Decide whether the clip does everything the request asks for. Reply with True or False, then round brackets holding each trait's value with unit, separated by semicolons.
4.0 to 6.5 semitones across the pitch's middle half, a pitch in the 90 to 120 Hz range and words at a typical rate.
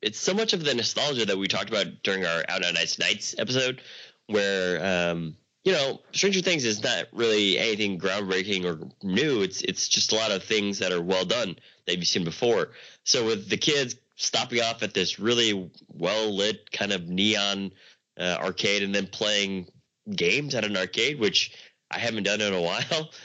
True (4.6 semitones; 100 Hz; 195 wpm)